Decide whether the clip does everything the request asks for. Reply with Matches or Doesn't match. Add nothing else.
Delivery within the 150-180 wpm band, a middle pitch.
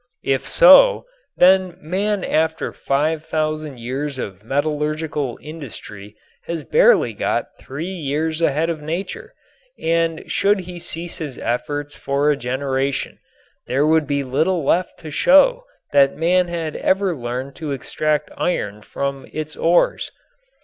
Doesn't match